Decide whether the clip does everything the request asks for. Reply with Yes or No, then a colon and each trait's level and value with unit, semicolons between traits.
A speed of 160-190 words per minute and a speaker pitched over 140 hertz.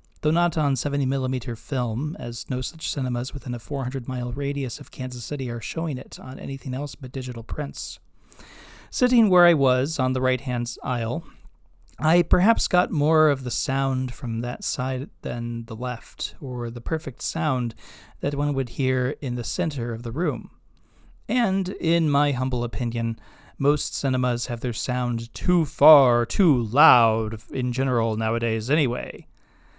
No: average, 165 wpm; low, 130 Hz